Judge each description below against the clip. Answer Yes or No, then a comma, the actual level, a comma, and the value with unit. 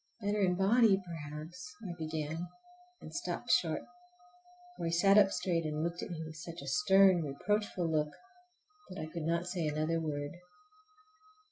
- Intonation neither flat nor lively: Yes, average, 3.1 semitones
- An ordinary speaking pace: Yes, average, 155 wpm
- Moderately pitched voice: Yes, medium, 170 Hz